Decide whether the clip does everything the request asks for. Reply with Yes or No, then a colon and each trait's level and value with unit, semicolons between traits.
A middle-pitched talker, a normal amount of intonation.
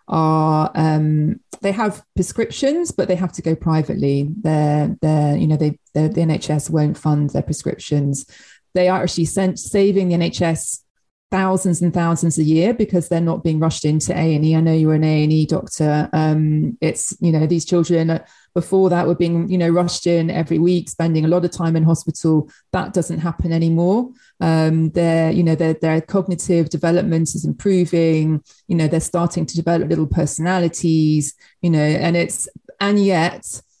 No: medium, 165 Hz; narrow, 2.1 semitones